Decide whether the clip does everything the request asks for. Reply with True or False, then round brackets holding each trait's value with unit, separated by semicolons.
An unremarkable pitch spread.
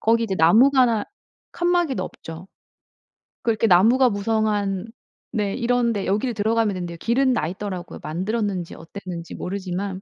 True (4.0 semitones)